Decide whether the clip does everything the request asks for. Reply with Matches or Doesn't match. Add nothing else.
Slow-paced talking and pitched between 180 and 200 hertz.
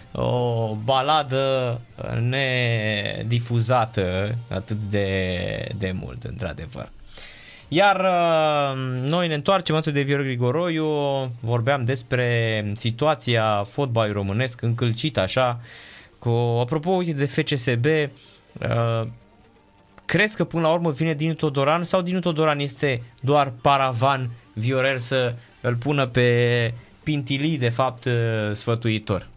Doesn't match